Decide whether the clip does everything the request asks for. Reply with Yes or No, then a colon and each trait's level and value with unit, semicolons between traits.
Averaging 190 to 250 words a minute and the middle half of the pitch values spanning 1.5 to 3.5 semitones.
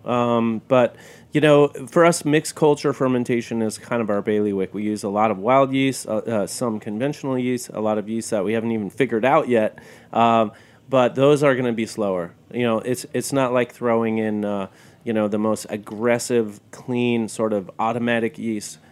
Yes: fast, 205 wpm; average, 2.8 semitones